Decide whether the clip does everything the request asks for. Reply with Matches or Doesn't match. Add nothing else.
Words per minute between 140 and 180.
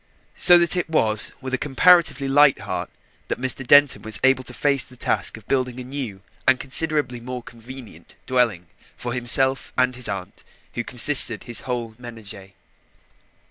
Matches